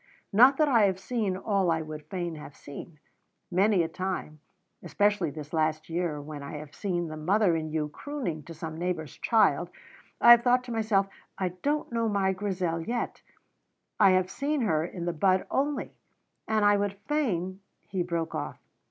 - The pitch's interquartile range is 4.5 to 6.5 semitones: Yes, average, 4.8 semitones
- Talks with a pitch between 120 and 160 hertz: No, medium, 185 Hz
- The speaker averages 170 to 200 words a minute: Yes, average, 185 wpm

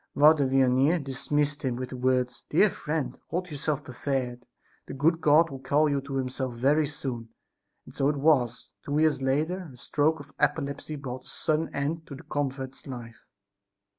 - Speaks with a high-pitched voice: No, medium, 140 Hz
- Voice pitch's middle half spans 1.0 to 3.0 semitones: Yes, narrow, 2.6 semitones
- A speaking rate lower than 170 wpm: No, average, 175 wpm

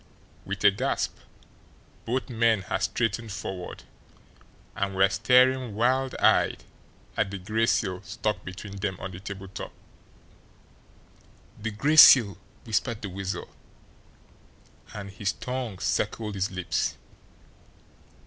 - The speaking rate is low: Yes, slow, 115 wpm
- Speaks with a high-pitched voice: No, low, 100 Hz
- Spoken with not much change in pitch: No, average, 3.2 semitones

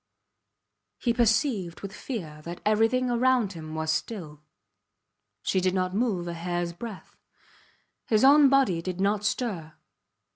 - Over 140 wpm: No, slow, 135 wpm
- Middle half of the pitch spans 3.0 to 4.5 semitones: No, wide, 5.5 semitones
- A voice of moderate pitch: No, high, 195 Hz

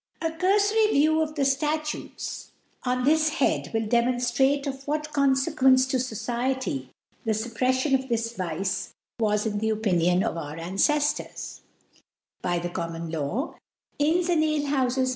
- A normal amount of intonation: No, wide, 5.8 semitones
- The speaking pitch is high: Yes, very high, 260 Hz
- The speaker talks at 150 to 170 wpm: No, average, 140 wpm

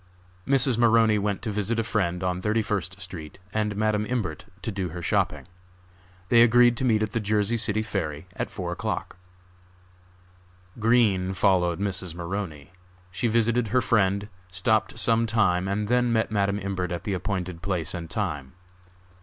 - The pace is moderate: Yes, average, 160 wpm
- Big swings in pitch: No, average, 3.5 semitones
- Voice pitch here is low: Yes, low, 105 Hz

